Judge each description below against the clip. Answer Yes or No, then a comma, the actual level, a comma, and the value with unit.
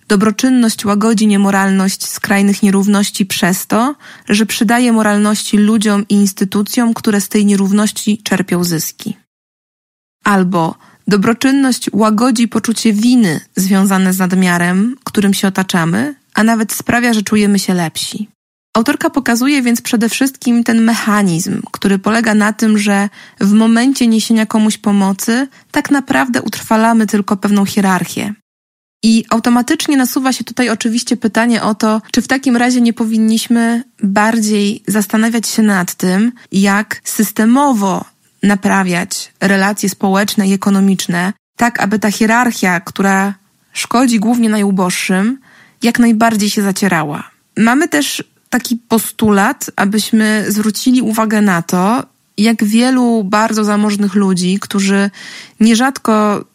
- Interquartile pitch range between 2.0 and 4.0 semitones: Yes, average, 2.7 semitones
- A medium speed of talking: Yes, average, 120 wpm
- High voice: Yes, high, 215 Hz